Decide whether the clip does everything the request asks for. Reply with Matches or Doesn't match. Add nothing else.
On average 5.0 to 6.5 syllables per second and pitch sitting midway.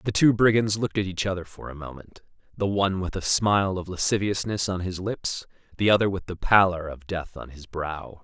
Doesn't match